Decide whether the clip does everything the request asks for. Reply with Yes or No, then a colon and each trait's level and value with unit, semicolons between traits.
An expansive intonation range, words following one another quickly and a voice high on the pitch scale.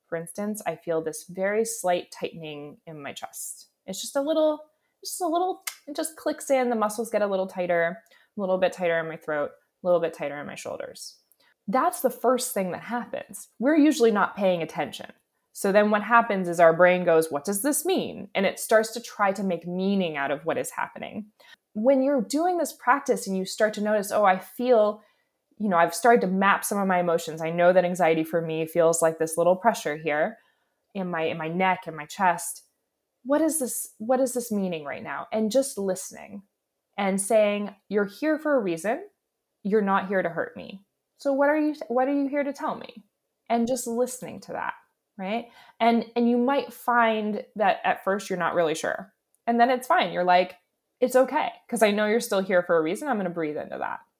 Yes: wide, 6.0 semitones; fast, 220 wpm; high, 210 Hz